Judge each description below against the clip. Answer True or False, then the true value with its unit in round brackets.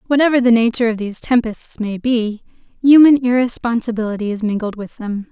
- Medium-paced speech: True (160 wpm)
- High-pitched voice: True (230 Hz)